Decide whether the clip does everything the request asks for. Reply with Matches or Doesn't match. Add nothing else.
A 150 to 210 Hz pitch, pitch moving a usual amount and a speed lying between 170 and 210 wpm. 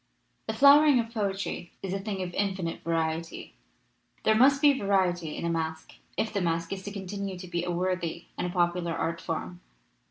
Matches